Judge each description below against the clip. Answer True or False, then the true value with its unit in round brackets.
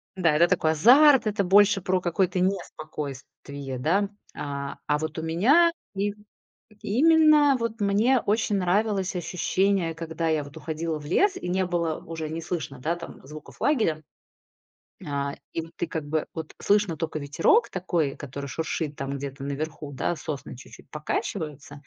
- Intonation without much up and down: False (4.9 semitones)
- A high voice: False (165 Hz)